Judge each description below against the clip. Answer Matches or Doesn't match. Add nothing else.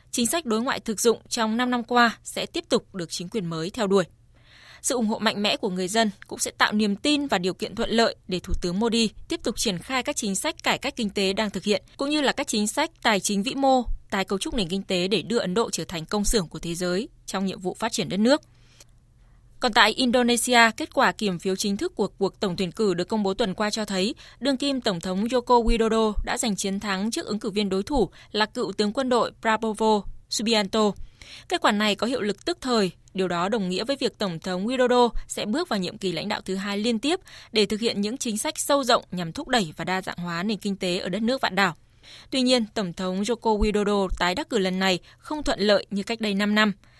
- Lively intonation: Doesn't match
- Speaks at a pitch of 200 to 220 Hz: Matches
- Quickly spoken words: Matches